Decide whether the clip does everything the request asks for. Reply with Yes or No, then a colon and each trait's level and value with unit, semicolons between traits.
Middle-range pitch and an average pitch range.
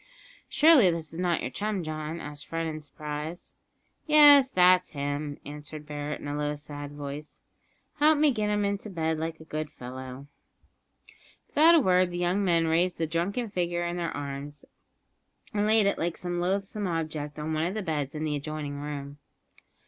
Yes: medium, 160 Hz; average, 3.8 semitones